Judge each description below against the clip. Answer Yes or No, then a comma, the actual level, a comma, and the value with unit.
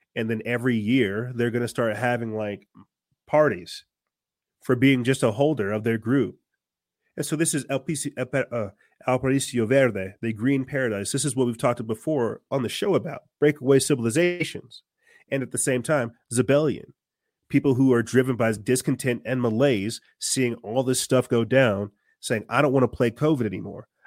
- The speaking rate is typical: Yes, average, 175 wpm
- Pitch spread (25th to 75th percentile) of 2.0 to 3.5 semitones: Yes, average, 3.1 semitones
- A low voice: Yes, low, 125 Hz